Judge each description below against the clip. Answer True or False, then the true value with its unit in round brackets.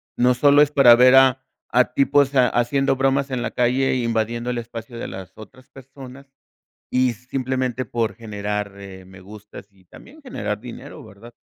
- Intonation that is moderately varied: True (3.4 semitones)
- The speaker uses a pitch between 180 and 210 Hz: False (125 Hz)